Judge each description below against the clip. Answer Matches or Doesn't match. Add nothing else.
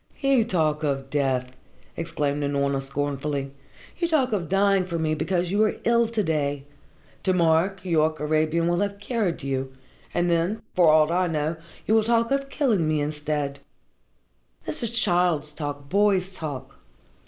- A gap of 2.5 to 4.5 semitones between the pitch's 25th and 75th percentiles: Doesn't match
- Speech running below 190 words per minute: Matches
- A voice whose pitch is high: Doesn't match